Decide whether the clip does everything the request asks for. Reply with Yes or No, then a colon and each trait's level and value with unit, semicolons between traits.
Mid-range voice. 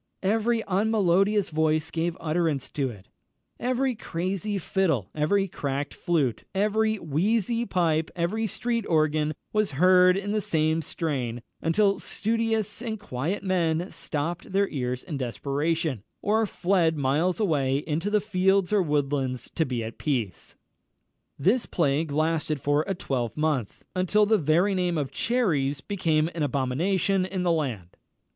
Yes: medium, 165 Hz